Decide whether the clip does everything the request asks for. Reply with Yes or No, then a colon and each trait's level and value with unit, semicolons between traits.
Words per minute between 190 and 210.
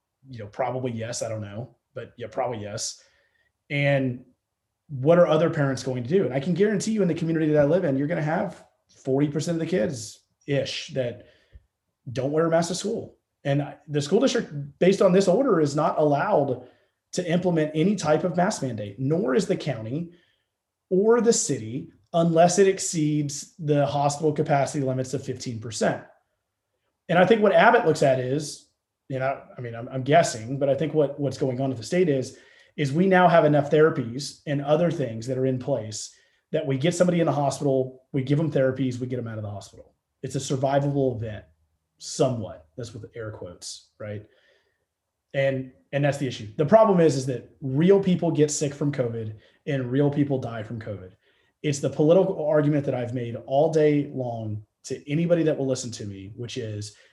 Yes: average, 200 wpm